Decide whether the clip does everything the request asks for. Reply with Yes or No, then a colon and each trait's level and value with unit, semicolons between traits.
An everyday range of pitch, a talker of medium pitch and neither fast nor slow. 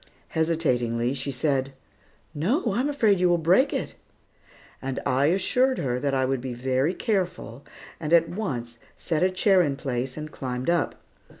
No: wide, 5.9 semitones; medium, 150 Hz; average, 165 wpm